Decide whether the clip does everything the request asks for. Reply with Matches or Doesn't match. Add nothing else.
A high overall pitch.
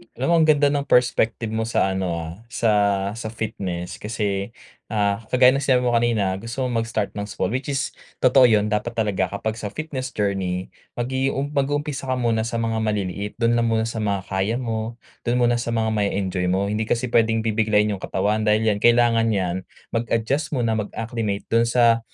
Doesn't match